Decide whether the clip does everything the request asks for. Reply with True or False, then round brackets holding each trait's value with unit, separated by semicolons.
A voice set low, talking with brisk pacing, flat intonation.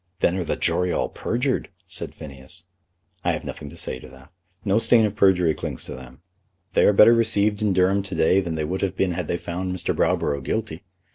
False (90 Hz; 220 wpm; 4.0 semitones)